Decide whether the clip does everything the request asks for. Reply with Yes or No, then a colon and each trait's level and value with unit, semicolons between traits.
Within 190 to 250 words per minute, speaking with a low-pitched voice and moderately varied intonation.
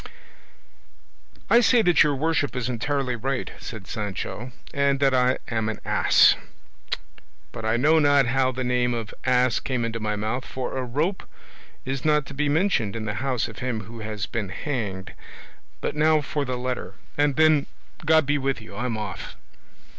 No: average, 180 wpm; low, 130 Hz; average, 4.1 semitones